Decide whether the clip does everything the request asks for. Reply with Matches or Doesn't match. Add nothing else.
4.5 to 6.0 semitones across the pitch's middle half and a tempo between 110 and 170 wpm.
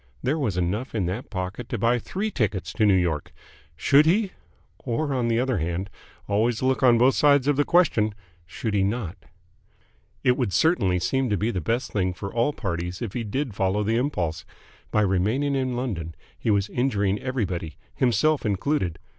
Doesn't match